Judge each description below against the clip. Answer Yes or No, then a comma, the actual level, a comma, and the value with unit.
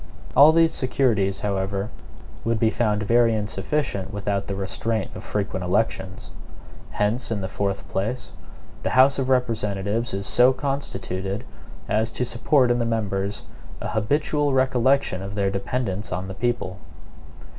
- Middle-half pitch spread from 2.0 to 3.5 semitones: No, average, 4.1 semitones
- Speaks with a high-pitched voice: No, low, 110 Hz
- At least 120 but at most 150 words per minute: Yes, average, 145 wpm